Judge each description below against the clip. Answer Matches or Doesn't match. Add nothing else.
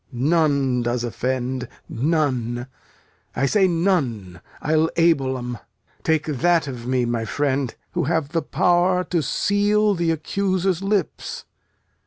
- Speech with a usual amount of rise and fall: Doesn't match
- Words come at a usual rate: Doesn't match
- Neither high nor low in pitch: Matches